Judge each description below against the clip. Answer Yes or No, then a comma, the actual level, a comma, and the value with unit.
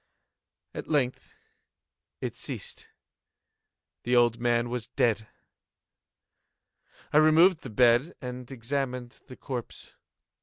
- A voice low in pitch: Yes, low, 125 Hz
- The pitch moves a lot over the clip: No, narrow, 2.5 semitones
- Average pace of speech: No, slow, 100 wpm